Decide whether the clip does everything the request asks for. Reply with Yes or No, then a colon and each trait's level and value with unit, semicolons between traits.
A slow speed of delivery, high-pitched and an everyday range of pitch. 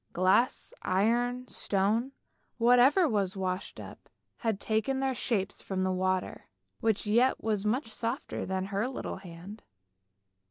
Yes: slow, 130 wpm; high, 215 Hz; average, 4.3 semitones